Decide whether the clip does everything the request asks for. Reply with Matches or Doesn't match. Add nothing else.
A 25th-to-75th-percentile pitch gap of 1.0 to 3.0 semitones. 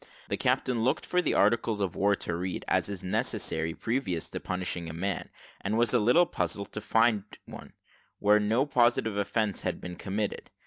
Doesn't match